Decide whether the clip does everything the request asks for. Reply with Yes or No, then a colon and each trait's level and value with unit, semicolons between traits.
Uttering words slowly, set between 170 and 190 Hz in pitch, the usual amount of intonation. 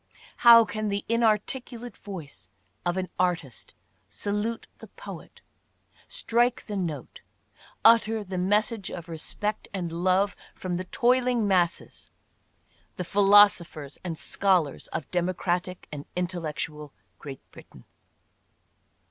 Yes: slow, 115 wpm; medium, 185 Hz; average, 3.9 semitones